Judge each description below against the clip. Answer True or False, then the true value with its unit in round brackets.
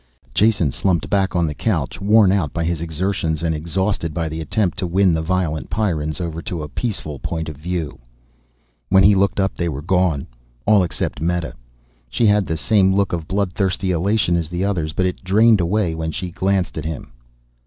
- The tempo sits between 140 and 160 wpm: False (200 wpm)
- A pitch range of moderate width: True (3.3 semitones)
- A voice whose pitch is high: False (90 Hz)